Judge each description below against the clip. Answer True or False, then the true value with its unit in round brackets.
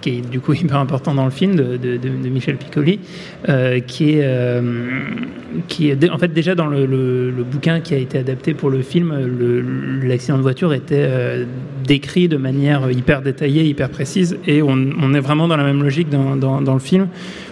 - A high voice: False (140 Hz)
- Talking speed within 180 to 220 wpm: True (210 wpm)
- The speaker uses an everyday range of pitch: True (3.8 semitones)